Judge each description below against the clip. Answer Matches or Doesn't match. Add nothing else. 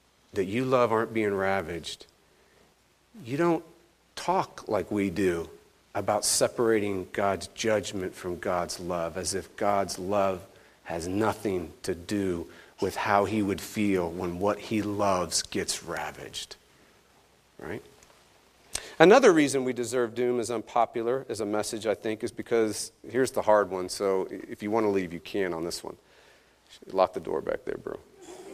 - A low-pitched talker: Matches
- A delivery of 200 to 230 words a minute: Doesn't match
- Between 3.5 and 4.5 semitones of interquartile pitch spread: Matches